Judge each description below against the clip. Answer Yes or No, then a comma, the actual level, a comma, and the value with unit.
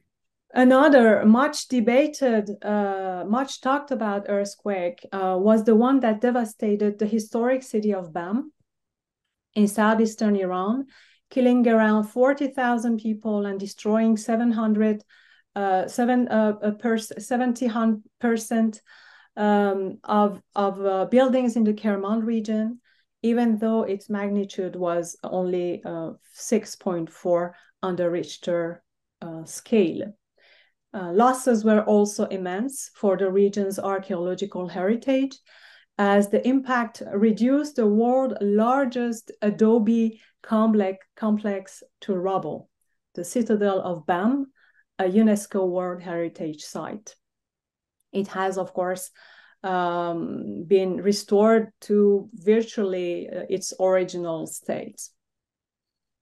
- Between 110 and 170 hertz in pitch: No, high, 210 Hz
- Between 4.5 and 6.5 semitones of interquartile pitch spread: No, average, 3.3 semitones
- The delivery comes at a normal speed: No, slow, 105 wpm